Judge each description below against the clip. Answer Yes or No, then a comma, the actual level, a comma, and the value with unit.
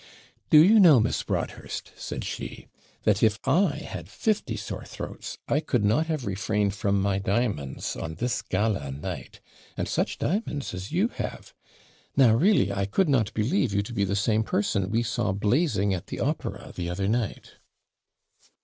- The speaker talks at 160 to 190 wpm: Yes, average, 170 wpm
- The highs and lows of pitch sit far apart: Yes, wide, 6.0 semitones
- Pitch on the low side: Yes, low, 110 Hz